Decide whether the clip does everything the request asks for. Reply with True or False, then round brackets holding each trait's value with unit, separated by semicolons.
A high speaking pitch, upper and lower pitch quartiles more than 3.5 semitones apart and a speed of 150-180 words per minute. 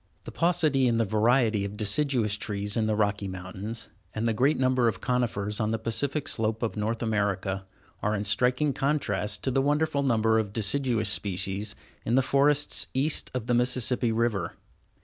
False (115 Hz; 3.9 semitones; 175 wpm)